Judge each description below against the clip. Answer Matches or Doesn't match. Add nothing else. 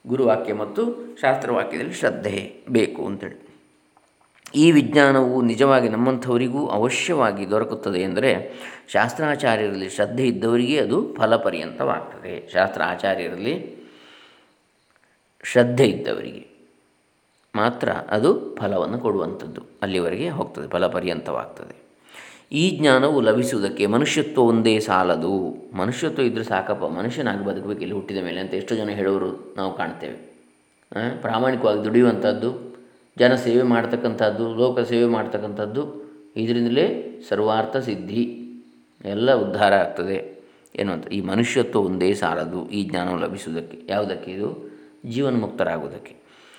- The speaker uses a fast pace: Doesn't match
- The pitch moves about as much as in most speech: Doesn't match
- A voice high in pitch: Doesn't match